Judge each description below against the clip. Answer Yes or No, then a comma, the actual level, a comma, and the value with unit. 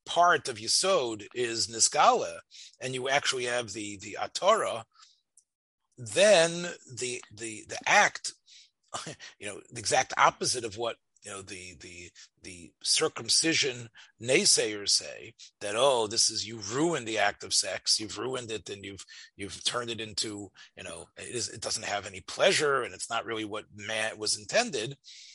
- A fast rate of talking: No, average, 160 wpm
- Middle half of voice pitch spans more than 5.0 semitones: No, average, 3.2 semitones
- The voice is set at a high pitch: No, low, 110 Hz